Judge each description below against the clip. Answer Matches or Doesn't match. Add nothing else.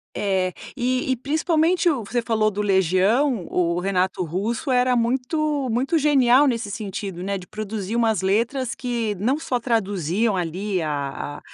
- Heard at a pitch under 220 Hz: Doesn't match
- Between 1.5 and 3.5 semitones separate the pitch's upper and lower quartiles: Doesn't match